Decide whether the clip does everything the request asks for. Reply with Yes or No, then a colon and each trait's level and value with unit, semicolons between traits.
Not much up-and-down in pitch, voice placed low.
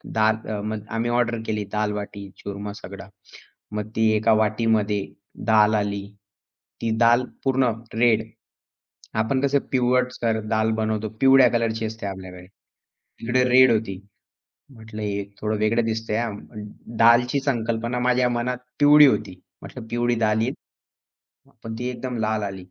Yes: narrow, 2.2 semitones; low, 110 Hz